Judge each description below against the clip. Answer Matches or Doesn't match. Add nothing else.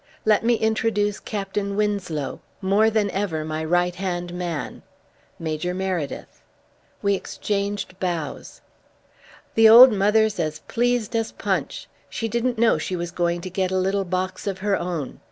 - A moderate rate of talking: Matches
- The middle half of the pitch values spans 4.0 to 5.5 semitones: Doesn't match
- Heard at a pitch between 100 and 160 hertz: Doesn't match